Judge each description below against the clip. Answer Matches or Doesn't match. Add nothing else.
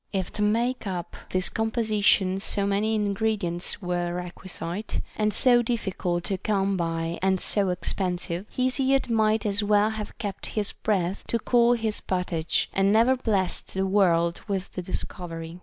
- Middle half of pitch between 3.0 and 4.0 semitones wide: Matches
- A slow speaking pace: Doesn't match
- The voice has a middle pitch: Doesn't match